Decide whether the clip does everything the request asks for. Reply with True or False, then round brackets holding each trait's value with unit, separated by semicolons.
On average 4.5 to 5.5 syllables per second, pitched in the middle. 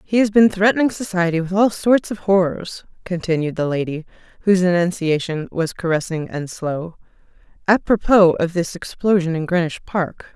True (5.2 syllables/s; 180 Hz)